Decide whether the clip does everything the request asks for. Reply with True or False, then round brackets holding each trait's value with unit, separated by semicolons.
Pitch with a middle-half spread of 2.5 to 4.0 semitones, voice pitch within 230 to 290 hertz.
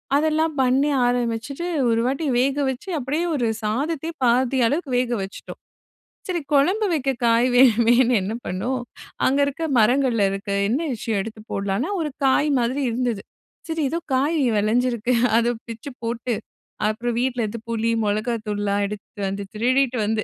True (3.7 semitones; 245 Hz)